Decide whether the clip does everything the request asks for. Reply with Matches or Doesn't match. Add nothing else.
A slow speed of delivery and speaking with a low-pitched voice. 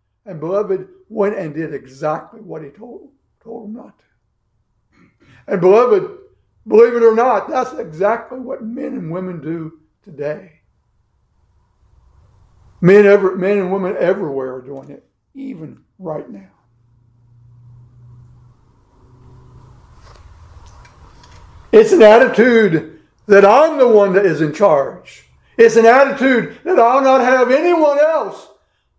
Doesn't match